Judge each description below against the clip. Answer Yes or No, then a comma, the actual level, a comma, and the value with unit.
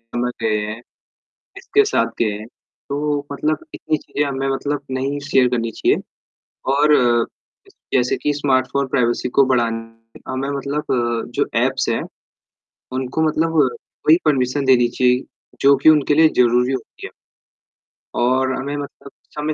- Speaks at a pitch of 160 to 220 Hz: No, low, 135 Hz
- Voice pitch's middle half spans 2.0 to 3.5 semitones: Yes, narrow, 2.6 semitones